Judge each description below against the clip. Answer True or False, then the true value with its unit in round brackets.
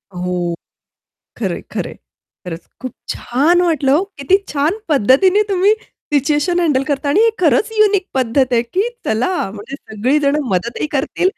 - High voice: True (280 Hz)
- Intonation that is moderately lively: False (6.7 semitones)